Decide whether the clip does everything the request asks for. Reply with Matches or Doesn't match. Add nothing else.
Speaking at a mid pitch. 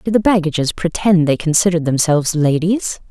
Matches